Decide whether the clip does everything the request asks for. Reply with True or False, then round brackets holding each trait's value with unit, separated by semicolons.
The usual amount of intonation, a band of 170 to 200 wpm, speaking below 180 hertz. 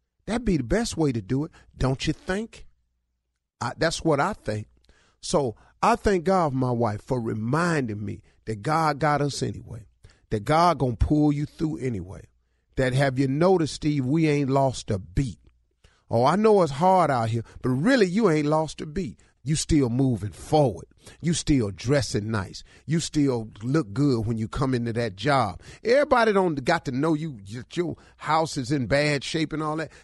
False (5.7 semitones; 190 wpm; 140 Hz)